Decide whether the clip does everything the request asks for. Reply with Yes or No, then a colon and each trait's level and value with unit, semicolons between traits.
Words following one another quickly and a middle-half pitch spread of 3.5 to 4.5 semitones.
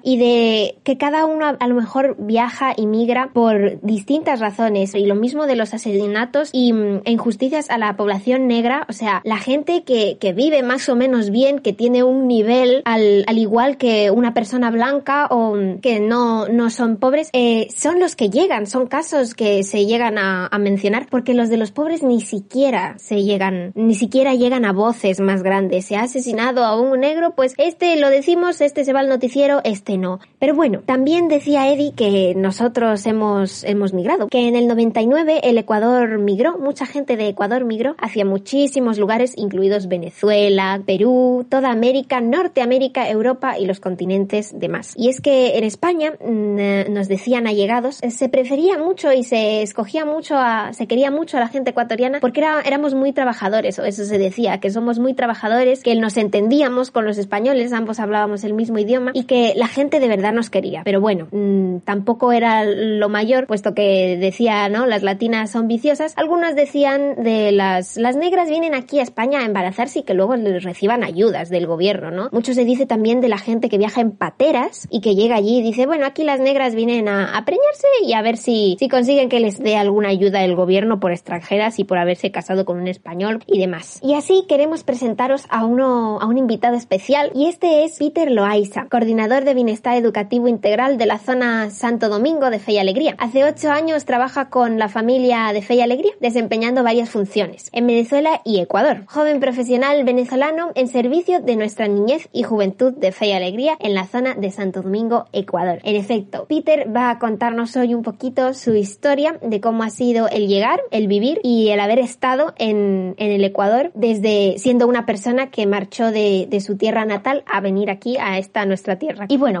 Yes: fast, 195 wpm; average, 4.2 semitones